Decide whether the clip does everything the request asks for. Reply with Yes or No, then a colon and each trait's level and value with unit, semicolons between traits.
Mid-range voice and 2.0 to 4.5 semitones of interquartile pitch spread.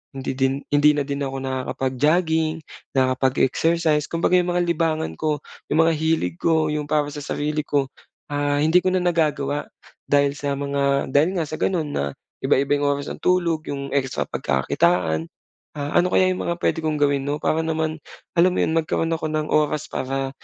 Yes: medium, 150 Hz; average, 2.7 semitones